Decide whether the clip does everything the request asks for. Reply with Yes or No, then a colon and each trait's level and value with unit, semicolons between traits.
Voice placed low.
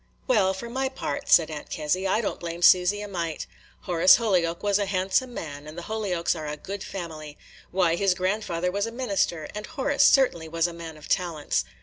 No: medium, 180 Hz